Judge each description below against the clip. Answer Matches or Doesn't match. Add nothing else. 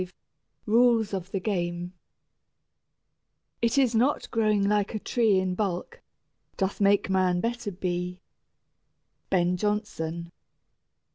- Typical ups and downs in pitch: Matches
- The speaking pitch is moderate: Doesn't match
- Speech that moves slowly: Matches